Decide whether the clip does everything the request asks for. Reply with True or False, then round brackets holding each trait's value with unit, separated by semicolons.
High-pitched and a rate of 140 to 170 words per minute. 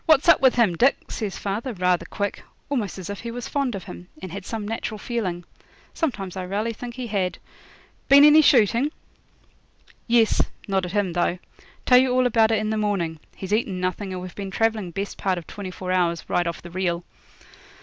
False (205 Hz; 205 wpm)